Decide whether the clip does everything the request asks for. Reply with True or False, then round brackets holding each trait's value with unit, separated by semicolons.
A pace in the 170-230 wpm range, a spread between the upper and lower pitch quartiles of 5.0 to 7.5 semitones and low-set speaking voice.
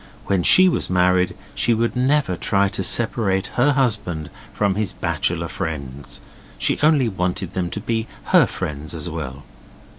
False (155 wpm; 5.4 semitones; 95 Hz)